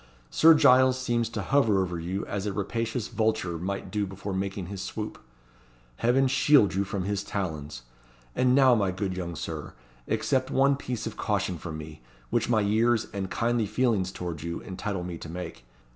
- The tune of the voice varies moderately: Yes, average, 4.7 semitones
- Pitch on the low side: Yes, low, 100 Hz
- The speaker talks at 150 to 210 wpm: Yes, average, 180 wpm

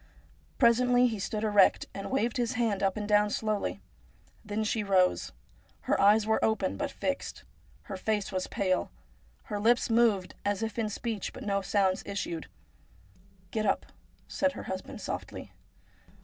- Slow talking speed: No, average, 165 wpm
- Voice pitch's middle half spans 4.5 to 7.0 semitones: No, narrow, 2.5 semitones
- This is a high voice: Yes, high, 210 Hz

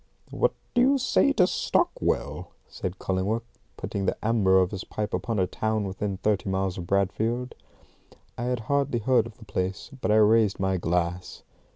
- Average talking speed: Yes, average, 175 wpm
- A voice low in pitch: Yes, low, 105 Hz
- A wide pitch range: No, average, 3.6 semitones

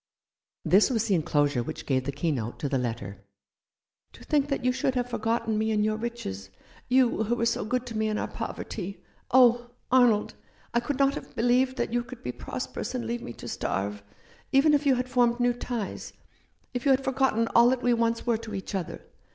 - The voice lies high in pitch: Yes, high, 235 Hz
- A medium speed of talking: No, fast, 215 wpm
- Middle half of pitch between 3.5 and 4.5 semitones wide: Yes, average, 4.2 semitones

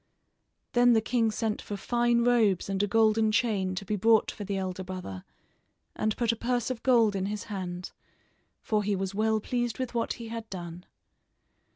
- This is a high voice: Yes, high, 215 Hz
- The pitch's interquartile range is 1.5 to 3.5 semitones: Yes, average, 3.2 semitones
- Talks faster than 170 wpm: Yes, average, 190 wpm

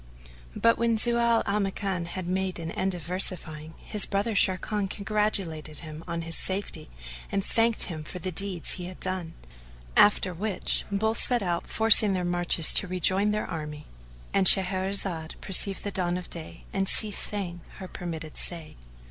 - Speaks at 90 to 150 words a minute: No, average, 165 wpm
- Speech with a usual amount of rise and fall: Yes, average, 3.1 semitones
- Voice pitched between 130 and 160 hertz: No, medium, 185 Hz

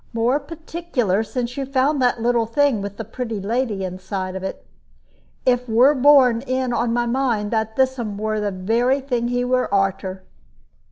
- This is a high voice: Yes, high, 240 Hz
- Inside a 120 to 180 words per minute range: Yes, average, 170 wpm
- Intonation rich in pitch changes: No, average, 3.7 semitones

